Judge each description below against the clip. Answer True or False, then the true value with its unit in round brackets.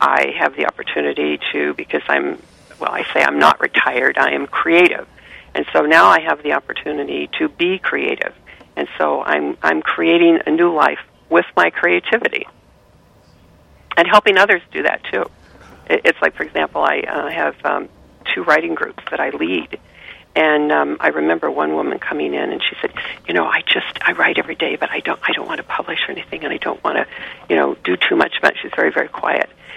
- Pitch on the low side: False (155 Hz)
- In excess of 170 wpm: True (205 wpm)